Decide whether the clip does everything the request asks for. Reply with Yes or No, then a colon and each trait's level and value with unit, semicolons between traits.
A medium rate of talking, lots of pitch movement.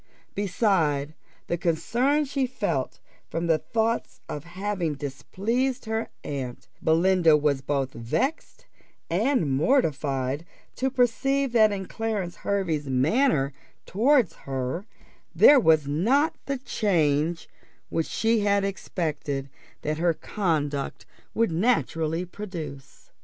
No: slow, 110 wpm; wide, 7.3 semitones